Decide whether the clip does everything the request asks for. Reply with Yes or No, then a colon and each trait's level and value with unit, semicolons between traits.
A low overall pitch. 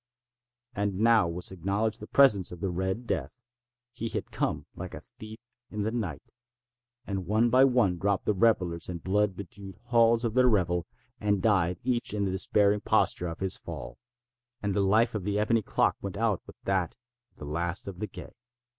Yes: low, 100 Hz